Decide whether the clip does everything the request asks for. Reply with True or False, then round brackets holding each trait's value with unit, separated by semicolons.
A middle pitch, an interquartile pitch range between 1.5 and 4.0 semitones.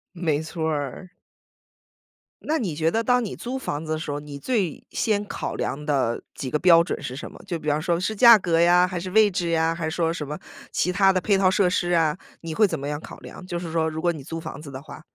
True (165 Hz; 3.4 semitones)